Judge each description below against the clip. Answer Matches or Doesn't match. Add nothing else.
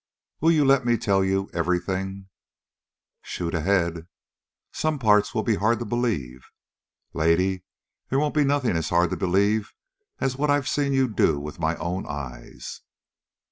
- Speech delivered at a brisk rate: Doesn't match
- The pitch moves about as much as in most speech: Doesn't match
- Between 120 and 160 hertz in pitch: Doesn't match